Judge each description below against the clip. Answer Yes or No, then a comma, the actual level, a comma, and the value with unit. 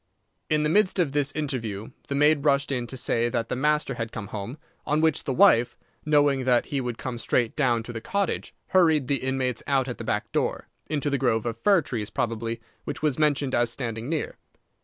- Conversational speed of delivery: No, fast, 215 wpm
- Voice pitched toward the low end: Yes, low, 130 Hz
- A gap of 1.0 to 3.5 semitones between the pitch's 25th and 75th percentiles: No, average, 4.0 semitones